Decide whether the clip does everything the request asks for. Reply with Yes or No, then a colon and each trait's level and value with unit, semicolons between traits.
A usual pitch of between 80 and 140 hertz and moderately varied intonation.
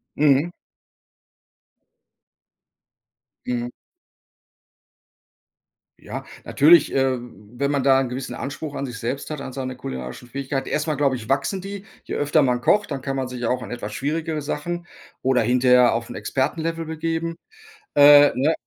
Yes: low, 135 Hz; average, 3.4 semitones